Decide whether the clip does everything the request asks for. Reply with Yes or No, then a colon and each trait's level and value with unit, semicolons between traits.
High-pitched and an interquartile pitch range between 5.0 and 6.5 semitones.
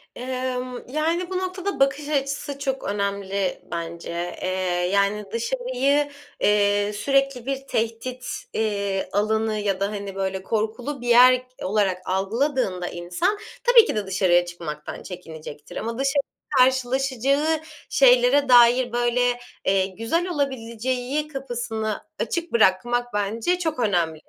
Yes: high, 240 Hz; average, 5.3 semitones